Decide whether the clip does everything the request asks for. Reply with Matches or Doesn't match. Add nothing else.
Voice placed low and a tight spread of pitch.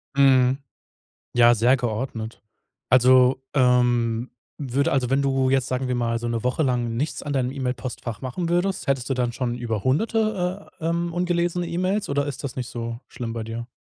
Doesn't match